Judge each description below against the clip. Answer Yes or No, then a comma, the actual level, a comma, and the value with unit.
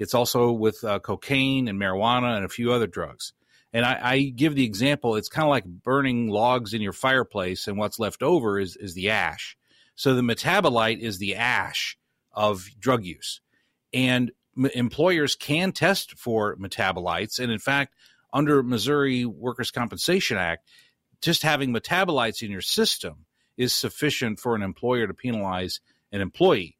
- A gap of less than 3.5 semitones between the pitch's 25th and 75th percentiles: No, average, 4.3 semitones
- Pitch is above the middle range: No, low, 120 Hz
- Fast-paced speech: No, average, 165 wpm